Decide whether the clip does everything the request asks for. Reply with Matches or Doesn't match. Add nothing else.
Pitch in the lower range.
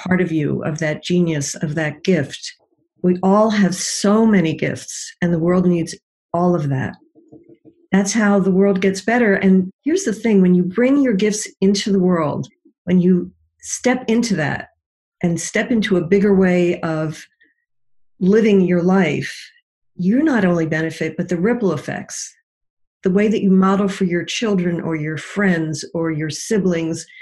Doesn't match